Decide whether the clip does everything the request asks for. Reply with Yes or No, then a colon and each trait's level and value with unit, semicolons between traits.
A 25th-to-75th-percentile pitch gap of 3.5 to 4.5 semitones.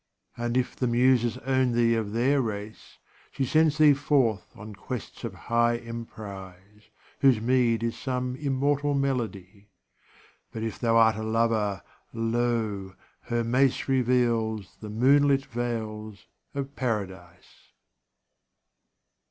No: average, 3.0 semitones